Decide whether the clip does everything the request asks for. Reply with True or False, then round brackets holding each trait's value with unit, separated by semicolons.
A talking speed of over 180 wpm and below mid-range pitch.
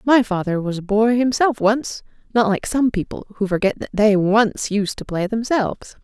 False (200 wpm; 215 Hz)